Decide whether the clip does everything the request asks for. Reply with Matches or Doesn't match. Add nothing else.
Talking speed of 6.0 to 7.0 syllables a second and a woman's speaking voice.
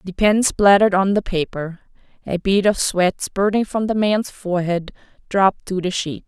Doesn't match